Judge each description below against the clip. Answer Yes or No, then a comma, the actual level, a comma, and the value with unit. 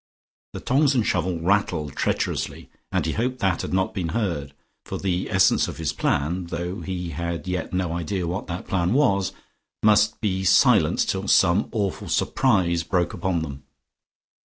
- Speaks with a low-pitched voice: Yes, very low, 90 Hz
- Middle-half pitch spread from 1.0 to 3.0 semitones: Yes, average, 2.7 semitones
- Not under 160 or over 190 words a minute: Yes, average, 165 wpm